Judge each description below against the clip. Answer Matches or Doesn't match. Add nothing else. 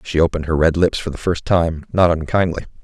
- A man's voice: Matches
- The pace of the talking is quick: Matches